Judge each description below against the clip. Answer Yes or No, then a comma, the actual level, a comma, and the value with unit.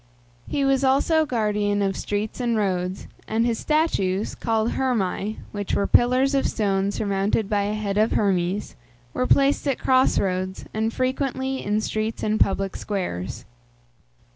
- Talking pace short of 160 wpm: Yes, average, 150 wpm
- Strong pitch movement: No, average, 4.4 semitones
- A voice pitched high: Yes, high, 215 Hz